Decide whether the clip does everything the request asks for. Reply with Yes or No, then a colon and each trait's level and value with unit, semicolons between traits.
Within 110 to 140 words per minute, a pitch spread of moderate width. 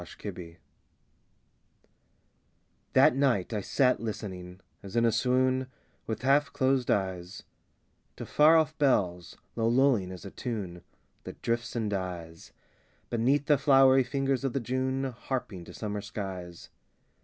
No: slow, 135 wpm; wide, 5.8 semitones